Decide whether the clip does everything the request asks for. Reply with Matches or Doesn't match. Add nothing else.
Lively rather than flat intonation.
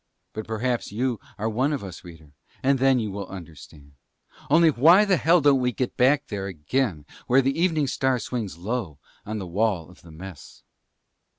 Matches